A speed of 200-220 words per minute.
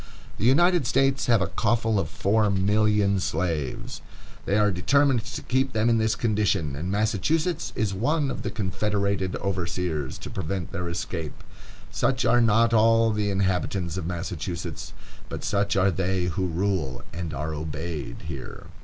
No: average, 160 wpm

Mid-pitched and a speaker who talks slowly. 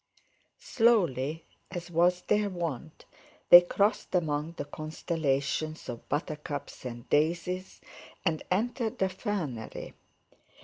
Yes: medium, 165 Hz; slow, 100 wpm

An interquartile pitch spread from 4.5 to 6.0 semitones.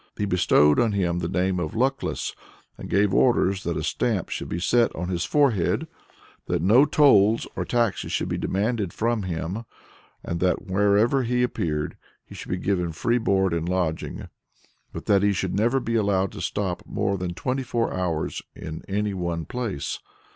Yes: average, 4.8 semitones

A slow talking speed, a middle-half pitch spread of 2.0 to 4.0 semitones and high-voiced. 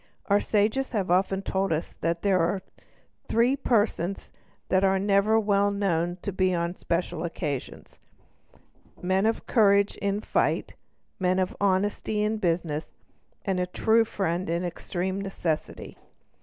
Yes: slow, 130 wpm; narrow, 2.6 semitones; high, 195 Hz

